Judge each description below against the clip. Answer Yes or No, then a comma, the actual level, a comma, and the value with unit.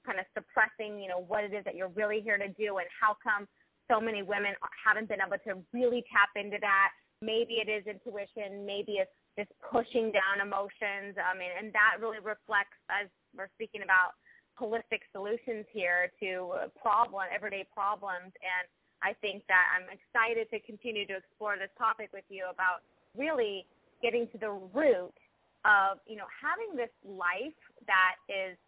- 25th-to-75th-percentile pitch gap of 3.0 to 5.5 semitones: No, narrow, 2.4 semitones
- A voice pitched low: No, high, 205 Hz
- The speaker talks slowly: No, average, 175 wpm